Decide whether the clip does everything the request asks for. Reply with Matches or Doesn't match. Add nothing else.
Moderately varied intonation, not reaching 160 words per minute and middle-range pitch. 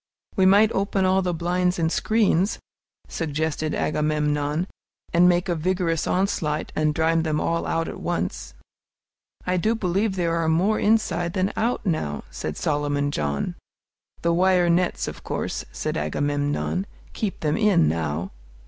Matches